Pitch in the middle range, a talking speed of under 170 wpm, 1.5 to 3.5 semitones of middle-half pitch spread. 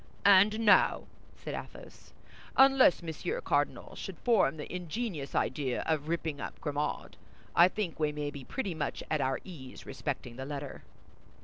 No: medium, 160 Hz; average, 150 wpm; wide, 5.6 semitones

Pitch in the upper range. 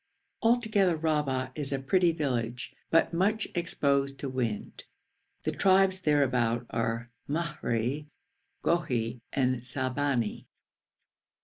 No: medium, 140 Hz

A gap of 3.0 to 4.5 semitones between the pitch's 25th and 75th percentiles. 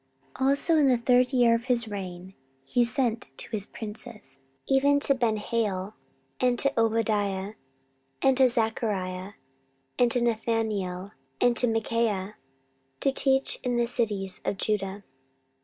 Yes: average, 3.4 semitones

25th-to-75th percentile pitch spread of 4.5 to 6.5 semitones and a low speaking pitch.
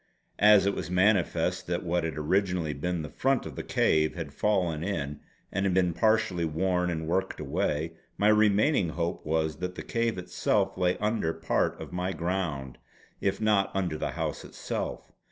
No: average, 3.6 semitones; very low, 90 Hz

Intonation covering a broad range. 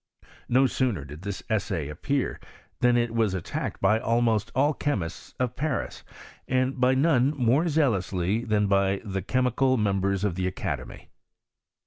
No: average, 4.9 semitones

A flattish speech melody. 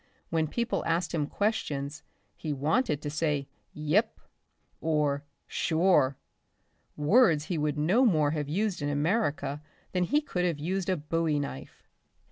No: average, 4.0 semitones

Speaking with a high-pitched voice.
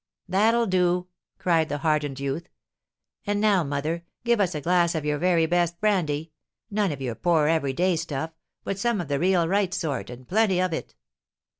No: medium, 170 Hz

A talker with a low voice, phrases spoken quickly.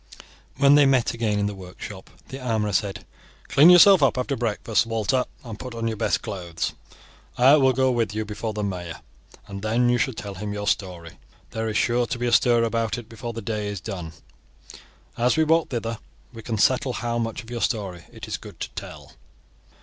Yes: low, 115 Hz; fast, 210 wpm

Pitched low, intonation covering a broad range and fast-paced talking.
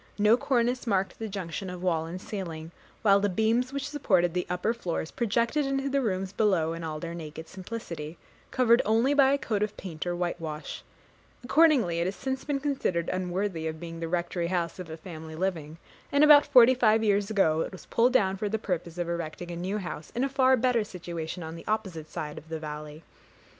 No: medium, 185 Hz; wide, 5.7 semitones; fast, 210 wpm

